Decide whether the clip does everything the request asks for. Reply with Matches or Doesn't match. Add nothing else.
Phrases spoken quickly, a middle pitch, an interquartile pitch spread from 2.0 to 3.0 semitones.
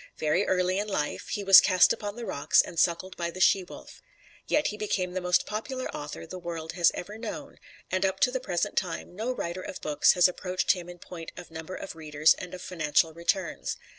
Matches